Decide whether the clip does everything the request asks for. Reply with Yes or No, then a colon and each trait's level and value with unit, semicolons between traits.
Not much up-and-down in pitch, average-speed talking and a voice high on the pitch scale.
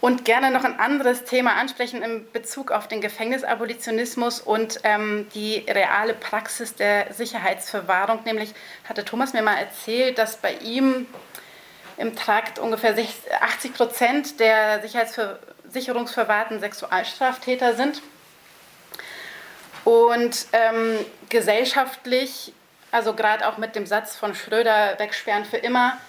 No: narrow, 2.3 semitones; slow, 115 wpm; high, 230 Hz